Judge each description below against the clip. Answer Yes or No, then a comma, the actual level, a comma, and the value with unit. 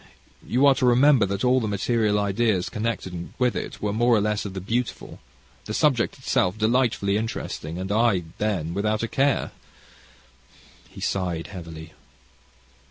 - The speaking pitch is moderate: No, low, 105 Hz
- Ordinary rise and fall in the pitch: Yes, average, 3.8 semitones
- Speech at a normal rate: Yes, average, 155 wpm